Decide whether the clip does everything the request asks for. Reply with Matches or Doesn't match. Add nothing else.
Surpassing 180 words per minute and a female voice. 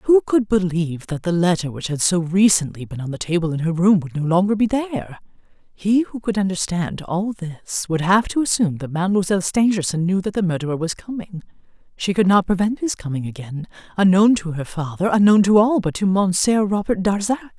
Matches